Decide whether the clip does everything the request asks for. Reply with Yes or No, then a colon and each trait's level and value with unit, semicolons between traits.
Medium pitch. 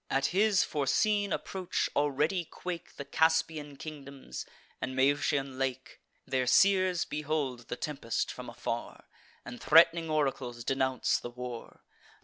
Yes: medium, 145 Hz